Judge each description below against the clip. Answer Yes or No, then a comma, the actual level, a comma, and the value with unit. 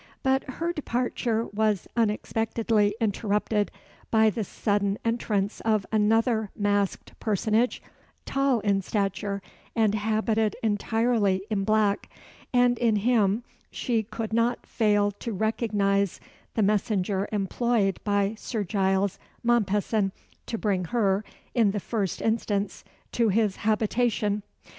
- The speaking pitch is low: No, high, 215 Hz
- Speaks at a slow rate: Yes, slow, 115 wpm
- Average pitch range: No, narrow, 2.0 semitones